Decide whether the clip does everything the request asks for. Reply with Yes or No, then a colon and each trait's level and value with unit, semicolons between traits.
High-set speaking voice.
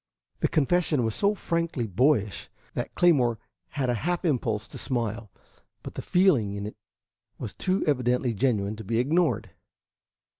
No: low, 125 Hz